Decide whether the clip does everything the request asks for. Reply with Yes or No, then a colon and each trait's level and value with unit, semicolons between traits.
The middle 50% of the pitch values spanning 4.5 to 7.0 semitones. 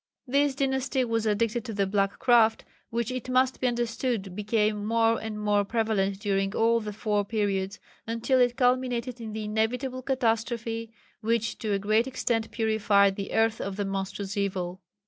No: average, 2.8 semitones